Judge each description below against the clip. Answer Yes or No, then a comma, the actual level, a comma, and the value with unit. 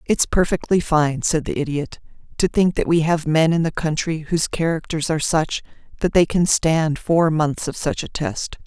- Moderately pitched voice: Yes, medium, 160 Hz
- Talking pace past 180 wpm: Yes, average, 200 wpm